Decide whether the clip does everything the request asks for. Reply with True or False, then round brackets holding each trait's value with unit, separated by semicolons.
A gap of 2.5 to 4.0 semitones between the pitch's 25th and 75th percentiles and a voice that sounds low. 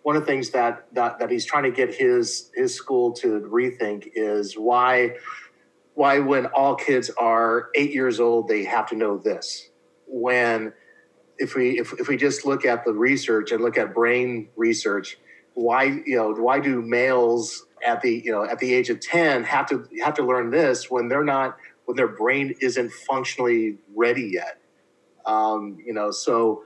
False (4.7 semitones; 125 Hz)